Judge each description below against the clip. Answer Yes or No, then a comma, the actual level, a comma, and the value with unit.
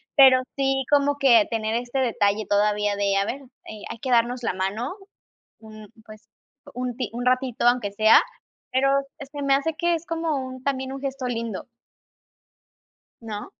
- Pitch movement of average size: Yes, average, 3.9 semitones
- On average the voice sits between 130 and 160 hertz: No, high, 245 Hz